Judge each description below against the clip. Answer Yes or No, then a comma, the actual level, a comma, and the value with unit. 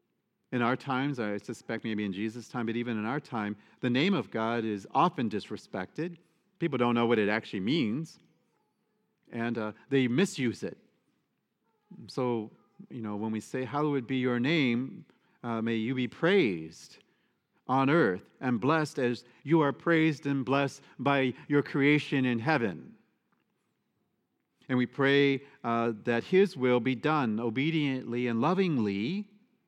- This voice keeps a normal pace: Yes, average, 150 wpm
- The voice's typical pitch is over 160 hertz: No, low, 130 Hz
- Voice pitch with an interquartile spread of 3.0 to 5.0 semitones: Yes, average, 4.1 semitones